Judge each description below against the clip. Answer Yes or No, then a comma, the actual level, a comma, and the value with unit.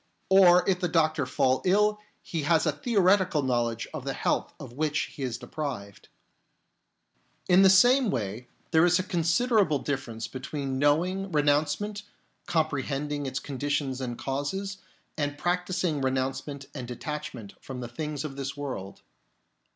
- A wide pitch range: No, average, 5.0 semitones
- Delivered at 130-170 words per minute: Yes, average, 150 wpm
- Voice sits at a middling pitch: Yes, medium, 150 Hz